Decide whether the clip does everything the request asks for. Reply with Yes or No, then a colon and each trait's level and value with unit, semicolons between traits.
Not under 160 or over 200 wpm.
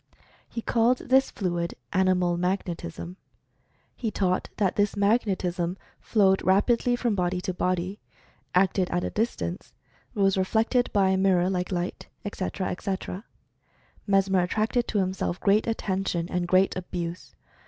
No: average, 140 wpm